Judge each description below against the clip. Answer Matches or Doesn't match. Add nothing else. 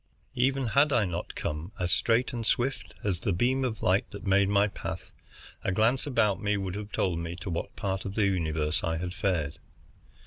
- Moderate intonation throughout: Matches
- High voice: Doesn't match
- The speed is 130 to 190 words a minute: Doesn't match